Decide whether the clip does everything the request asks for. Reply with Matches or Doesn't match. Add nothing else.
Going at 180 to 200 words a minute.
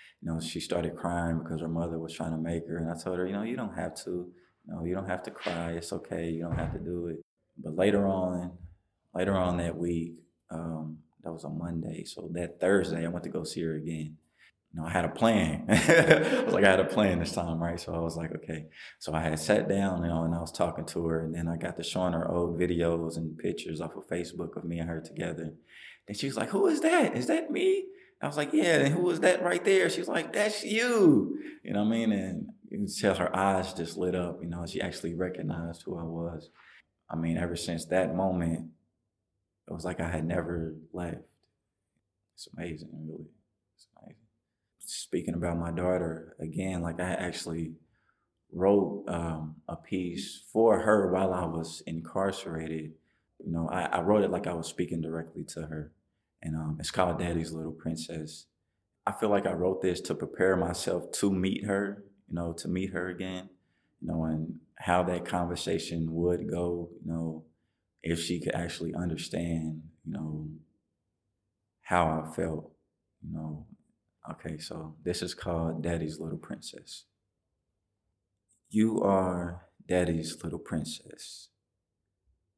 Matches